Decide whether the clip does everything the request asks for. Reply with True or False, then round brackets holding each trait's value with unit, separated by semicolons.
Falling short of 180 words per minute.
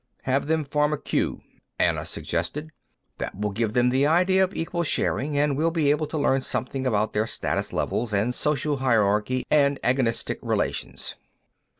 True (170 wpm)